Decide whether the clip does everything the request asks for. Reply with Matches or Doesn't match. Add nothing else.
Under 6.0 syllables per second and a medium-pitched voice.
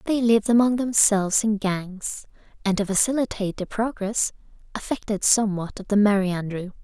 Doesn't match